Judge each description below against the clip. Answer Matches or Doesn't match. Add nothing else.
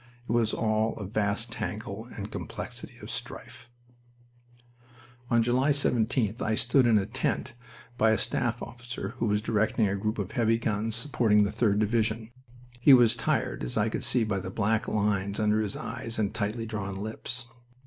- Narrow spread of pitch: Matches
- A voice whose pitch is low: Matches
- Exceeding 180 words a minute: Doesn't match